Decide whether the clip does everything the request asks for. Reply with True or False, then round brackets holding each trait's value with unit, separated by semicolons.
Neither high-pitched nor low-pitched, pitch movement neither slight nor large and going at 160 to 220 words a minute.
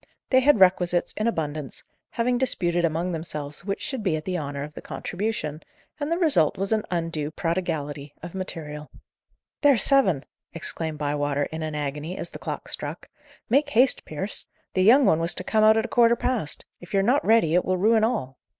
False (175 Hz; 6.4 semitones; 195 wpm)